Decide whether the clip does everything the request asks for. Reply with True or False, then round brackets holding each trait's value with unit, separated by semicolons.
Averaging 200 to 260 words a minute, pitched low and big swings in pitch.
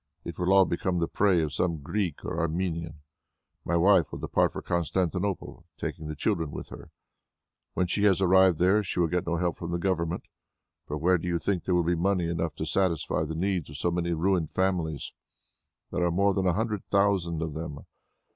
False (205 wpm; 85 Hz; 2.4 semitones)